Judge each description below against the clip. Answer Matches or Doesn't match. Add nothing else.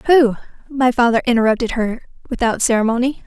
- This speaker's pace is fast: Doesn't match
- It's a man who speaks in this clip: Doesn't match